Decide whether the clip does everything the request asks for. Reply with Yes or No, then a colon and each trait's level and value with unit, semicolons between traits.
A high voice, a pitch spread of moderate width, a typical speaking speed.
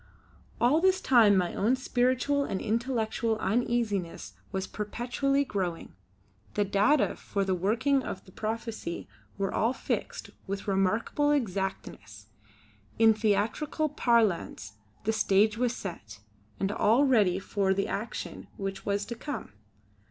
No: high, 215 Hz; average, 4.1 semitones; slow, 130 wpm